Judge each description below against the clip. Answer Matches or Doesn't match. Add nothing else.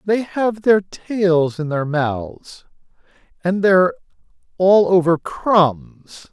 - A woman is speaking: Doesn't match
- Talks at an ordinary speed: Doesn't match